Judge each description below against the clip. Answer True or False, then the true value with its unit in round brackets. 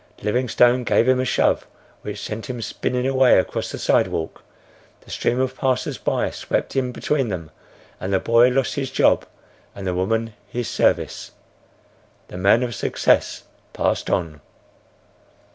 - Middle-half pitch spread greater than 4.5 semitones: False (4.2 semitones)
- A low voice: True (120 Hz)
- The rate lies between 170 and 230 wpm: False (150 wpm)